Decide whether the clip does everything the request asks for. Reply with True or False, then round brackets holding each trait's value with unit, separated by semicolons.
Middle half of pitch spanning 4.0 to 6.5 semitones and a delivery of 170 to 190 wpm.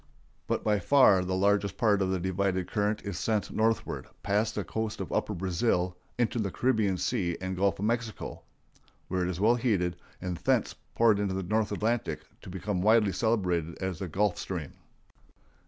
False (3.0 semitones; 180 wpm)